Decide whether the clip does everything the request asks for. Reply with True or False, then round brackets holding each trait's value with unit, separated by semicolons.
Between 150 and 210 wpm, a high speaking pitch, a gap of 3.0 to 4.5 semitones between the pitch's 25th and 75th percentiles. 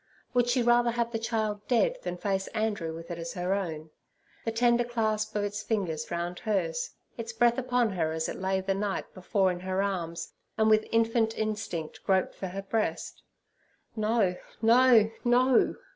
True (175 wpm; 210 Hz; 3.8 semitones)